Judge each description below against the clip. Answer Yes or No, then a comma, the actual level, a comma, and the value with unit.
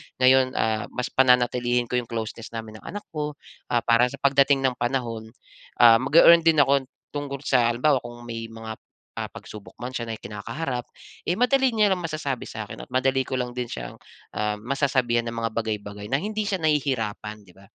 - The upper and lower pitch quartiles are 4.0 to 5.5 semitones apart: No, average, 3.5 semitones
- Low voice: Yes, low, 125 Hz